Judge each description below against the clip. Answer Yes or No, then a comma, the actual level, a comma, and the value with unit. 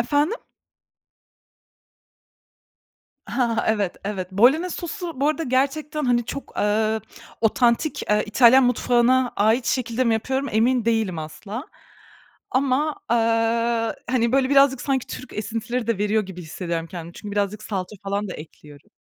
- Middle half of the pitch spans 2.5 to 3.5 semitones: No, average, 3.9 semitones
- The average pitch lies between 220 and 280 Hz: Yes, high, 230 Hz